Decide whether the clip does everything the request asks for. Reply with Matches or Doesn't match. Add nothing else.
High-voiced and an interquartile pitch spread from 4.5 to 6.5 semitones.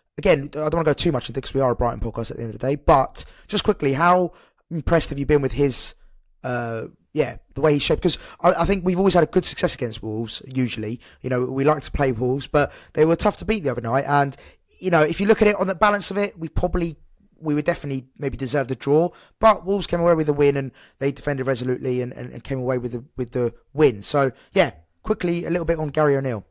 Doesn't match